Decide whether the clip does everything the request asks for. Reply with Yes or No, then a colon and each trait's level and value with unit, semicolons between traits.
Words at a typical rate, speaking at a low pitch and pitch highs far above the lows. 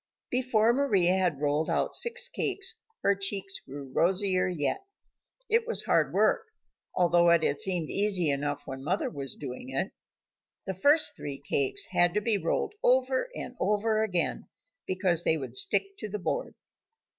No: average, 160 wpm; high, 190 Hz; wide, 6.9 semitones